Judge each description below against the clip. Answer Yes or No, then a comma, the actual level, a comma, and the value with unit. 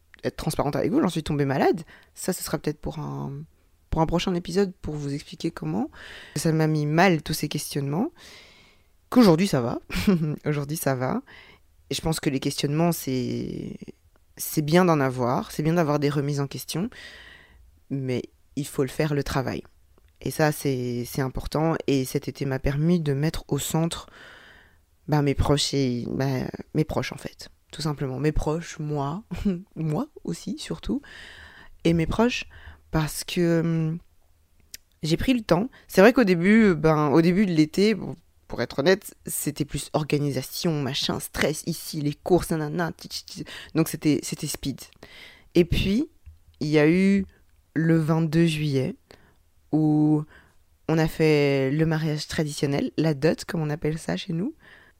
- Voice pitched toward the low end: No, medium, 150 Hz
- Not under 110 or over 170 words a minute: Yes, average, 165 wpm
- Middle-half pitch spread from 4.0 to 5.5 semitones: No, average, 3.4 semitones